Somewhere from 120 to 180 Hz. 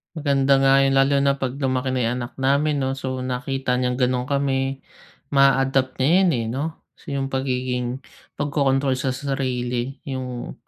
Yes: low, 135 Hz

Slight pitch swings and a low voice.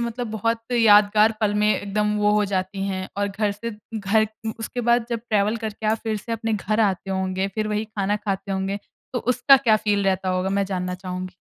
No: narrow, 2.2 semitones; high, 210 Hz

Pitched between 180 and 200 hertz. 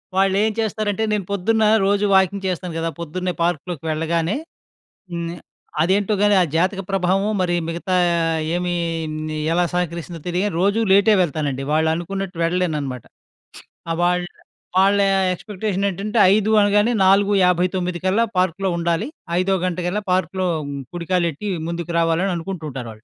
Yes: medium, 185 Hz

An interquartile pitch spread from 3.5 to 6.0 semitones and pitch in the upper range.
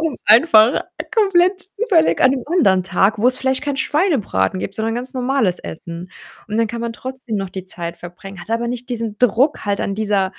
Yes: average, 5.3 semitones; high, 230 Hz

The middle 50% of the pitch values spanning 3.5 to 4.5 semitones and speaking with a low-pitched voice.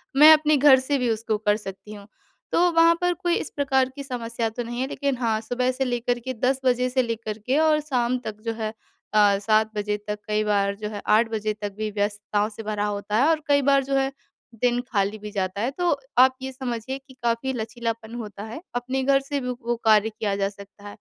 No: average, 3.9 semitones; high, 235 Hz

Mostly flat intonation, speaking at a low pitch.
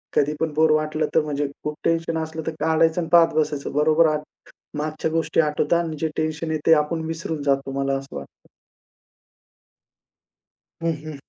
No: narrow, 1.4 semitones; medium, 155 Hz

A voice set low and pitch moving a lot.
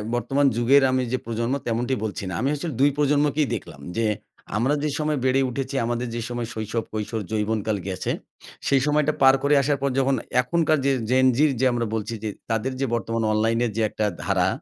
No: low, 125 Hz; average, 3.6 semitones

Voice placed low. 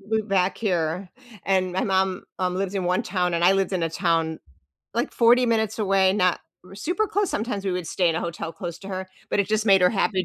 No: high, 190 Hz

